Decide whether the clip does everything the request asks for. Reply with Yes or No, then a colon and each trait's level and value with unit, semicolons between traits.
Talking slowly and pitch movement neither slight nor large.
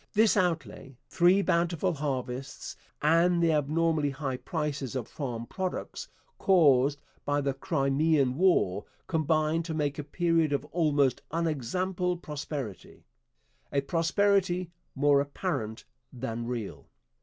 Yes: slow, 115 wpm; average, 3.8 semitones